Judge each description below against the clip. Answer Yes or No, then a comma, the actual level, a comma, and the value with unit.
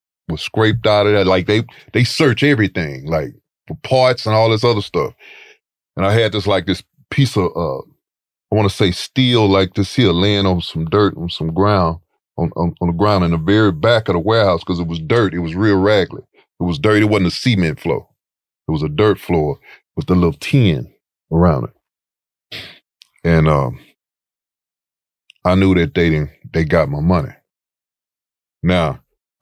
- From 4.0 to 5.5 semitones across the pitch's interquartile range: Yes, average, 4.3 semitones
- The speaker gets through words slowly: No, average, 190 wpm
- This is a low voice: Yes, very low, 95 Hz